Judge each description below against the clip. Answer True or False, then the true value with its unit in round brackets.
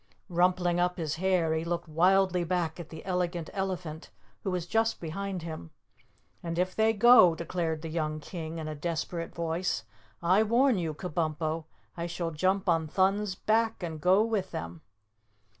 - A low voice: False (175 Hz)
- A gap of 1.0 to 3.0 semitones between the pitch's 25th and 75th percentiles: True (2.7 semitones)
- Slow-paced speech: False (165 wpm)